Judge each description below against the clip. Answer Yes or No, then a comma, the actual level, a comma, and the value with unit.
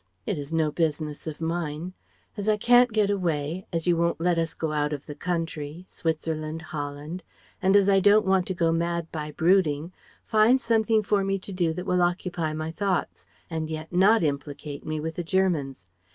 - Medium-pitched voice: Yes, medium, 165 Hz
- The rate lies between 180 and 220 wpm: Yes, average, 195 wpm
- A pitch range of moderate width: Yes, average, 3.5 semitones